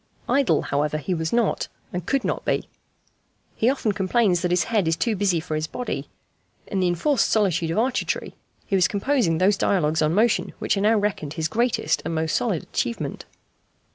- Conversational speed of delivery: Yes, average, 190 wpm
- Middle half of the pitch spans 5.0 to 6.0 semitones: Yes, wide, 5.5 semitones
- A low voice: No, high, 190 Hz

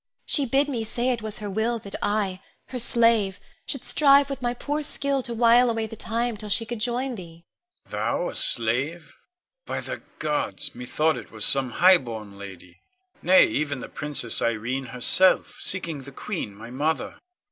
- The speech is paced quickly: No, average, 180 wpm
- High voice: Yes, high, 200 Hz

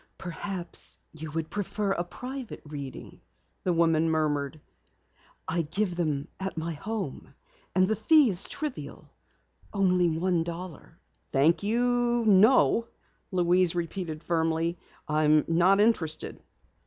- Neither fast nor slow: No, slow, 115 wpm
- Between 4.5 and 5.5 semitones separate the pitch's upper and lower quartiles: No, average, 4.1 semitones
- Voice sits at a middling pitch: Yes, medium, 175 Hz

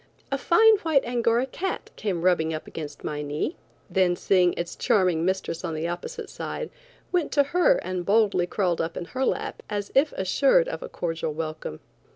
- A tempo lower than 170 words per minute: No, average, 185 wpm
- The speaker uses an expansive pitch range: Yes, wide, 8.5 semitones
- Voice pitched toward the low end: No, high, 190 Hz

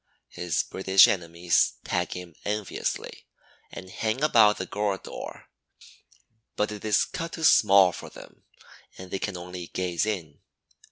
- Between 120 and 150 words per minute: Yes, average, 145 wpm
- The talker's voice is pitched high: No, very low, 95 Hz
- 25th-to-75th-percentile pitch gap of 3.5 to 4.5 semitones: No, average, 3.0 semitones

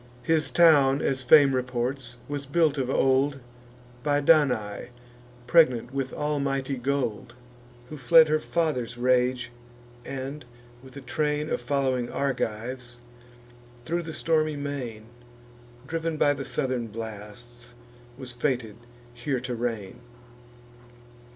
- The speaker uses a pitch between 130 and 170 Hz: Yes, low, 135 Hz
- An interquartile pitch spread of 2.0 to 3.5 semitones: Yes, average, 3.1 semitones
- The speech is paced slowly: Yes, slow, 115 wpm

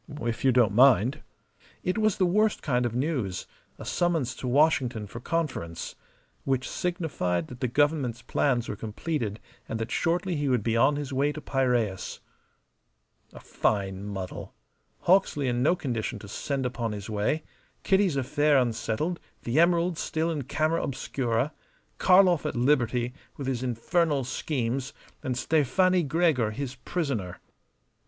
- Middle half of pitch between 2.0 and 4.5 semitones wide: No, average, 5.2 semitones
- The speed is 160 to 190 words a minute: No, average, 145 wpm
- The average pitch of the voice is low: Yes, low, 130 Hz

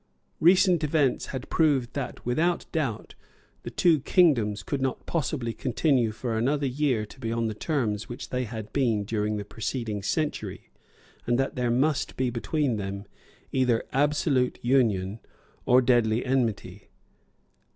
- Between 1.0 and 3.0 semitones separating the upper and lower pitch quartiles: No, average, 4.3 semitones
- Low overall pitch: Yes, low, 125 Hz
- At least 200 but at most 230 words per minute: No, average, 150 wpm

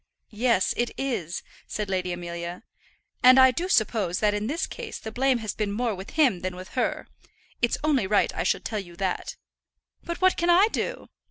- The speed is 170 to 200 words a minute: Yes, average, 195 wpm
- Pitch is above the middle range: Yes, high, 220 Hz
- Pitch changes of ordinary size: No, wide, 6.1 semitones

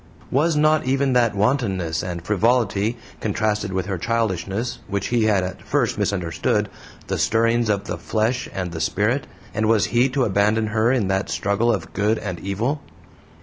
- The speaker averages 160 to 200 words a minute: Yes, average, 170 wpm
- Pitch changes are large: No, average, 3.6 semitones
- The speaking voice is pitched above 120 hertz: No, low, 110 Hz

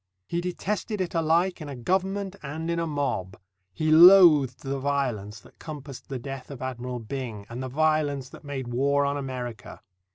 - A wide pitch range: No, average, 4.2 semitones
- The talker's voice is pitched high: No, medium, 140 Hz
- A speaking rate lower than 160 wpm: No, average, 175 wpm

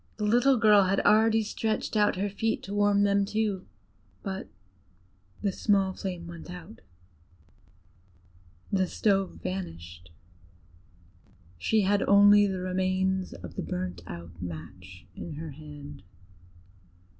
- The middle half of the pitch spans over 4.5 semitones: Yes, wide, 5.6 semitones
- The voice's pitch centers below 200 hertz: Yes, high, 190 Hz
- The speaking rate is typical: No, slow, 120 wpm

